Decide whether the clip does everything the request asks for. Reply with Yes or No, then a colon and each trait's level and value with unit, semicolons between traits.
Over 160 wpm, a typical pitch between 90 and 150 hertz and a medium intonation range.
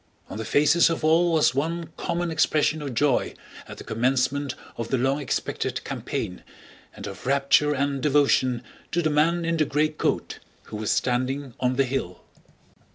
Yes: average, 170 wpm; medium, 140 Hz; average, 3.5 semitones